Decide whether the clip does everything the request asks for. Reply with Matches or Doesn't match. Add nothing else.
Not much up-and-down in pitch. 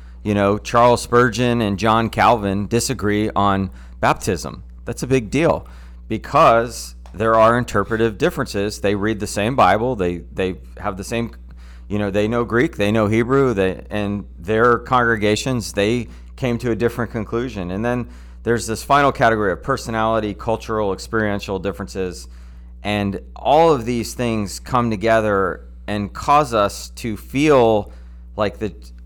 Doesn't match